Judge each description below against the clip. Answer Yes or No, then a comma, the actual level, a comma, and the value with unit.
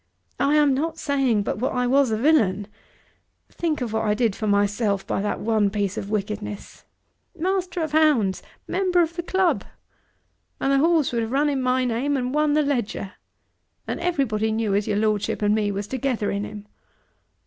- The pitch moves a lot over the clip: Yes, wide, 6.0 semitones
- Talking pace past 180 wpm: Yes, average, 190 wpm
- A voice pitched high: Yes, high, 245 Hz